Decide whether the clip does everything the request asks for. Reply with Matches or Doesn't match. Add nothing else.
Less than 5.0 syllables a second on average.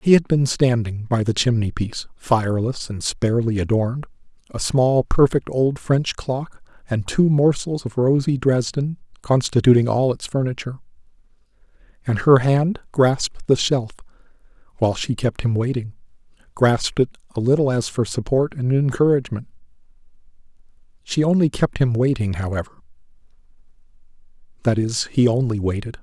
Doesn't match